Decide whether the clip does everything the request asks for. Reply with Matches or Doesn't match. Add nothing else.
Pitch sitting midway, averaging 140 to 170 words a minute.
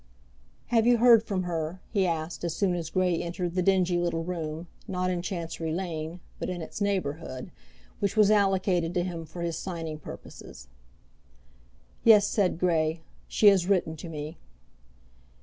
Matches